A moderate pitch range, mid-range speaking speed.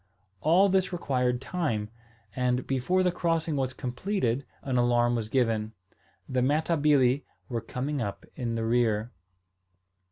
No: average, 4.3 semitones; slow, 130 wpm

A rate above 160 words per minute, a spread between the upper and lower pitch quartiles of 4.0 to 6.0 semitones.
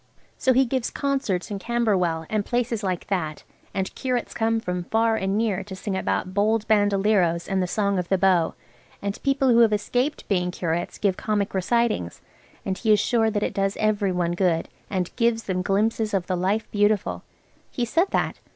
No: average, 190 wpm; average, 3.4 semitones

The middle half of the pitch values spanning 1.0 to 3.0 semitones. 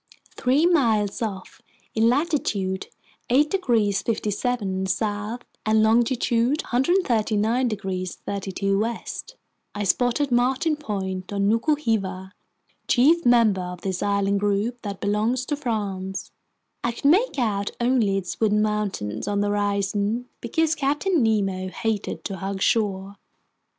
No: average, 3.8 semitones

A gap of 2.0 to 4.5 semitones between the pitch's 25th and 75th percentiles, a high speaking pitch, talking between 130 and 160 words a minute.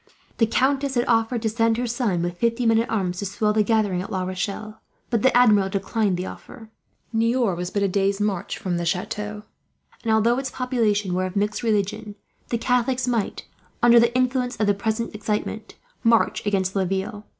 No: average, 3.0 semitones; high, 215 Hz; average, 195 wpm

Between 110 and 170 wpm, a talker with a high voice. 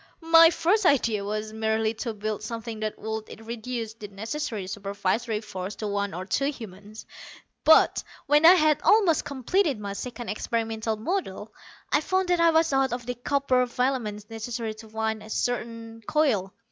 Yes: average, 165 wpm; high, 225 Hz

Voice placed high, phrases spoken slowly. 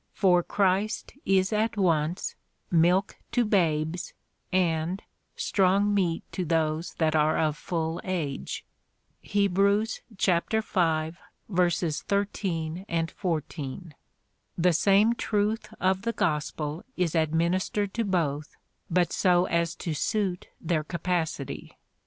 No: medium, 180 Hz; slow, 110 wpm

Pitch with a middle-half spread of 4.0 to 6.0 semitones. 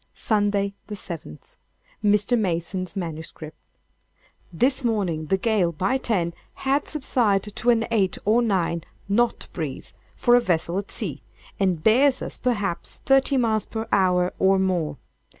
Yes: average, 4.5 semitones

